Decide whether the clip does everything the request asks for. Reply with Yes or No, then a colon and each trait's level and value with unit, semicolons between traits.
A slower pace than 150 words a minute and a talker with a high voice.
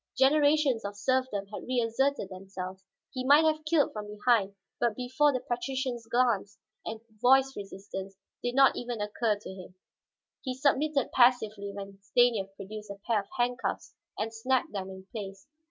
No: average, 155 wpm; high, 230 Hz